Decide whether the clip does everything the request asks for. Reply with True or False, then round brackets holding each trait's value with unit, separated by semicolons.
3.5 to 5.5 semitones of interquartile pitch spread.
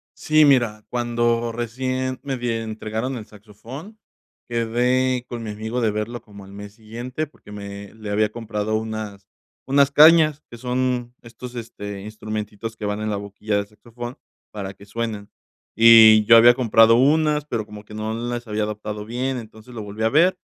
False (2.7 semitones)